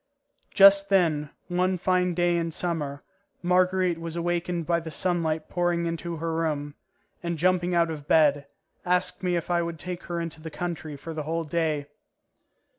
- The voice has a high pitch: No, medium, 170 Hz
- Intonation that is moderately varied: No, narrow, 1.9 semitones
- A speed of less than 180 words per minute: Yes, average, 170 wpm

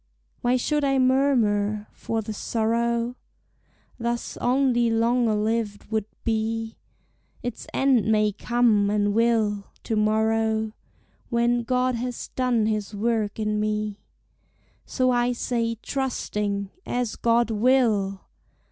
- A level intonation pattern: Yes, narrow, 2.3 semitones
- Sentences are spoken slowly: Yes, slow, 115 wpm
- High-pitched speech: Yes, high, 225 Hz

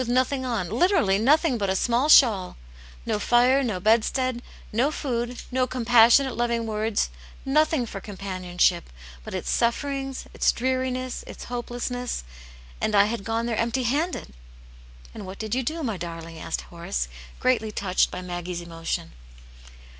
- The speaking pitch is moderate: No, high, 235 Hz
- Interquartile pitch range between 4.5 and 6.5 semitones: Yes, average, 5.1 semitones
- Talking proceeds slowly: No, average, 150 wpm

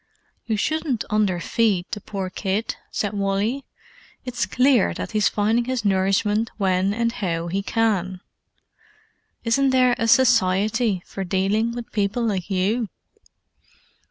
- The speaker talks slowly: Yes, slow, 130 wpm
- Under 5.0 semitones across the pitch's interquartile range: Yes, average, 3.3 semitones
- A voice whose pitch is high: Yes, high, 210 Hz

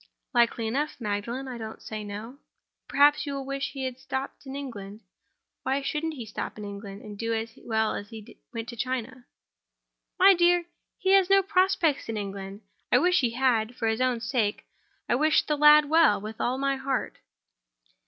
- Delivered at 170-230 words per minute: Yes, average, 190 wpm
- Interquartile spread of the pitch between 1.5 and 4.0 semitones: No, average, 4.6 semitones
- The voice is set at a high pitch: Yes, very high, 255 Hz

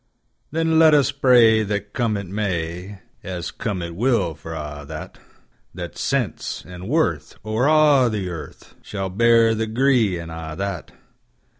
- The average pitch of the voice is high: No, low, 105 Hz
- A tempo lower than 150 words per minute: Yes, average, 140 wpm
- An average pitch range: No, wide, 5.7 semitones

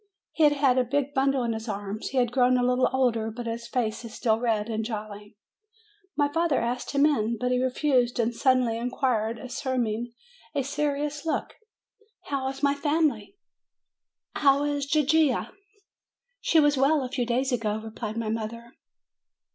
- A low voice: No, very high, 250 Hz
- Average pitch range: Yes, average, 3.6 semitones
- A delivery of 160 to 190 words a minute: Yes, average, 170 wpm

